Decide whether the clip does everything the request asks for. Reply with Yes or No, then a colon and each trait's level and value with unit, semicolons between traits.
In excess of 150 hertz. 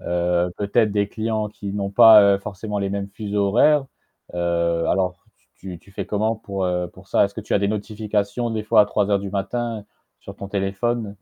No: low, 100 Hz